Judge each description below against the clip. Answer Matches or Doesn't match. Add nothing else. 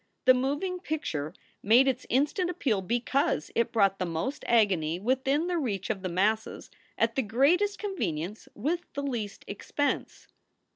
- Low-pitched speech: Doesn't match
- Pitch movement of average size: Doesn't match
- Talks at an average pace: Matches